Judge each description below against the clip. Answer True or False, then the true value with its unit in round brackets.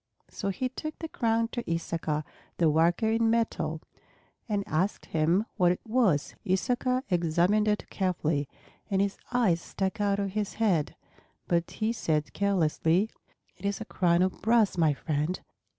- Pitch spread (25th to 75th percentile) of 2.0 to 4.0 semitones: False (4.8 semitones)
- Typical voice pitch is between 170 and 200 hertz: True (190 Hz)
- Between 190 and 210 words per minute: False (155 wpm)